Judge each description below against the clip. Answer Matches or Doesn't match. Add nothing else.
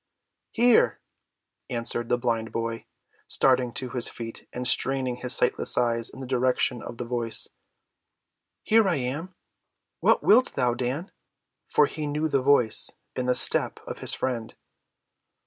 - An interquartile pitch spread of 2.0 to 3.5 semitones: Matches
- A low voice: Matches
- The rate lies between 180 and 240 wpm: Doesn't match